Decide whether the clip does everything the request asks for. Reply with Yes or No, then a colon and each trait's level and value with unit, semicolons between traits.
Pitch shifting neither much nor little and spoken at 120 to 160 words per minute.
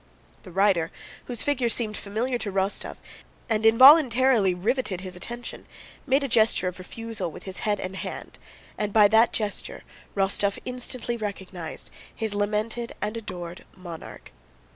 Yes: average, 3.8 semitones; average, 140 wpm